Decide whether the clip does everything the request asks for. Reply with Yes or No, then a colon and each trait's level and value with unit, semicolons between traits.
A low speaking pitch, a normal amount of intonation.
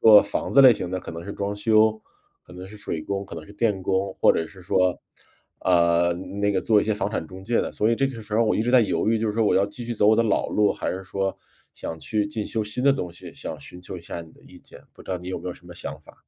Yes: low, 100 Hz; average, 3.1 semitones